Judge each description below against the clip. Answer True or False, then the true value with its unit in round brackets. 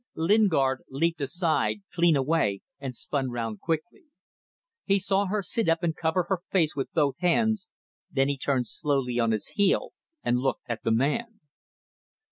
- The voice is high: False (160 Hz)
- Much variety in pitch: True (5.9 semitones)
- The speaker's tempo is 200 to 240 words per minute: False (160 wpm)